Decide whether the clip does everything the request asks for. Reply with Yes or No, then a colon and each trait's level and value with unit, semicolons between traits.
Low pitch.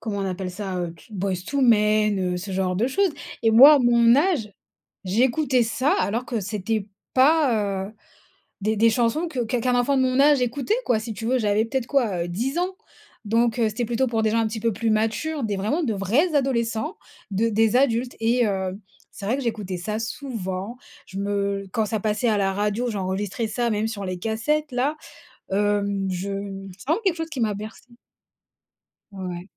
No: high, 220 Hz